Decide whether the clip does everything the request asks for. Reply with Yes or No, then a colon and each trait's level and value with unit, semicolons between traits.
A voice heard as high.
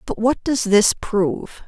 Yes: high, 215 Hz